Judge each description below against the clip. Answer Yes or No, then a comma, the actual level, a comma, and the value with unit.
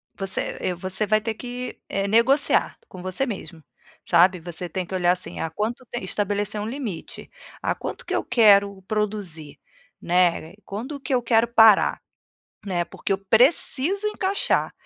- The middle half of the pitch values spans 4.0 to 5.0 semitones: Yes, average, 4.5 semitones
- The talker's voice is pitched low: No, high, 205 Hz